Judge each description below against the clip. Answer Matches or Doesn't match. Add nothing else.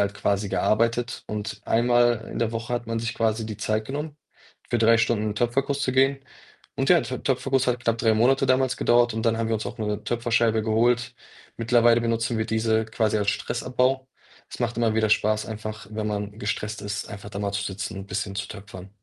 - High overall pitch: Doesn't match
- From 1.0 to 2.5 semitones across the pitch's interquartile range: Matches